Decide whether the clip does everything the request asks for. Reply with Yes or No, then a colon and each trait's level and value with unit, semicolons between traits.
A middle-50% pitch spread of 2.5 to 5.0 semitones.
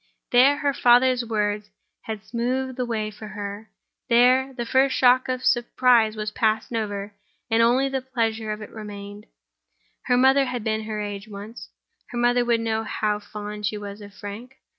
Yes: average, 3.0 semitones